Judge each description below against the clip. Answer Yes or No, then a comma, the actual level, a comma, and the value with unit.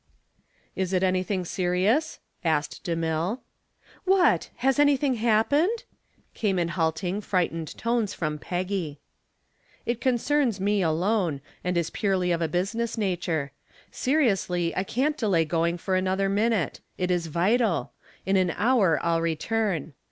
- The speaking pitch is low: No, medium, 185 Hz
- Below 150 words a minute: Yes, slow, 135 wpm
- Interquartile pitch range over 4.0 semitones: Yes, average, 5.0 semitones